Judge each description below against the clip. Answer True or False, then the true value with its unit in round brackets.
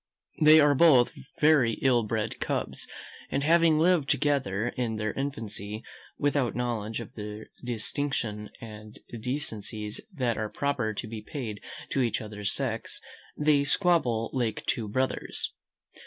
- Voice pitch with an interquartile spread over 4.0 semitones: True (4.7 semitones)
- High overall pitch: False (120 Hz)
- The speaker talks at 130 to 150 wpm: True (135 wpm)